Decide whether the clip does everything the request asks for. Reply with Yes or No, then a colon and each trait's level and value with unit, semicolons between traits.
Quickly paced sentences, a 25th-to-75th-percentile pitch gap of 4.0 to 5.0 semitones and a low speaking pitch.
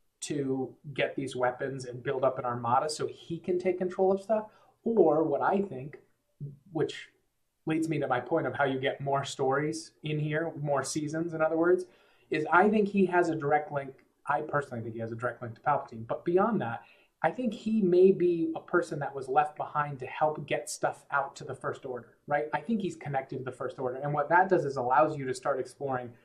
No: fast, 225 wpm; average, 4.5 semitones; medium, 150 Hz